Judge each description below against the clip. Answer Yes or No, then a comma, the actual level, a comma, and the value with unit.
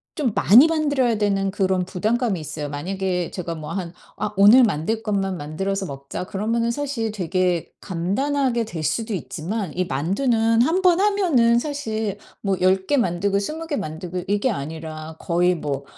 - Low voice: No, high, 195 Hz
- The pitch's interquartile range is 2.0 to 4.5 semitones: No, average, 5.1 semitones